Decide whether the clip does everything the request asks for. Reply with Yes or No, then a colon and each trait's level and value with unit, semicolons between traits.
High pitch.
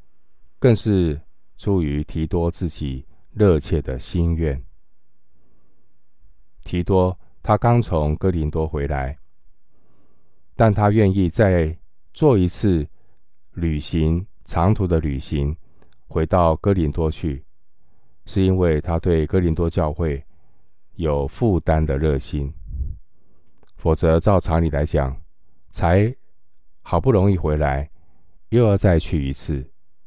No: very low, 80 Hz